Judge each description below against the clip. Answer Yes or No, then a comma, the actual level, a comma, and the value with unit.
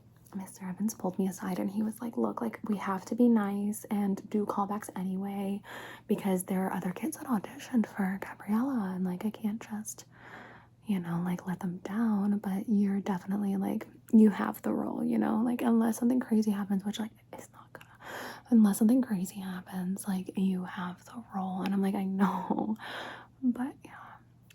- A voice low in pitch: No, high, 200 Hz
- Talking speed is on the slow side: No, average, 185 wpm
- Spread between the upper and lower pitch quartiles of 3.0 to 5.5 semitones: No, narrow, 2.5 semitones